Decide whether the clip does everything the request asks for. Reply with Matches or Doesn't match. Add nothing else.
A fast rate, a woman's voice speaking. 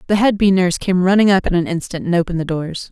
Matches